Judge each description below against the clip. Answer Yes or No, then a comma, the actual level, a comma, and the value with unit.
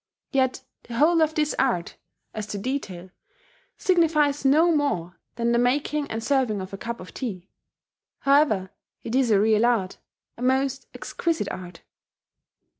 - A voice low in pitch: No, very high, 250 Hz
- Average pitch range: No, wide, 5.7 semitones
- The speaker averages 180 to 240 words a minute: No, average, 150 wpm